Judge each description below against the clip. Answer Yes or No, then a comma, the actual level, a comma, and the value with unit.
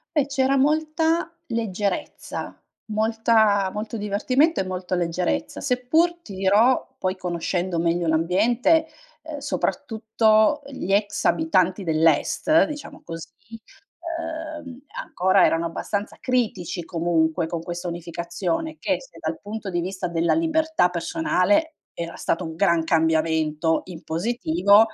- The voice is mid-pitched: No, high, 200 Hz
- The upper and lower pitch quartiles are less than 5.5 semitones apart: No, wide, 7.3 semitones